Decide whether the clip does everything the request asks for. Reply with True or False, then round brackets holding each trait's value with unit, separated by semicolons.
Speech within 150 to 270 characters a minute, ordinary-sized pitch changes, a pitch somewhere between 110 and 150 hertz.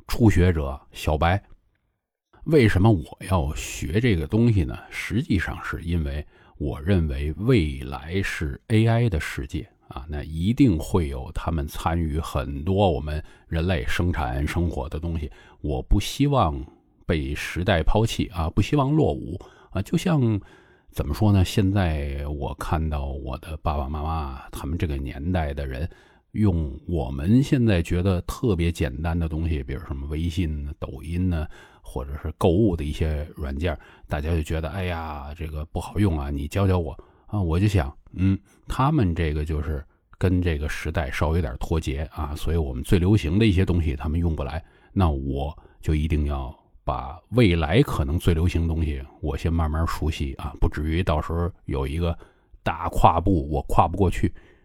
False (255 characters per minute; 4.1 semitones; 85 Hz)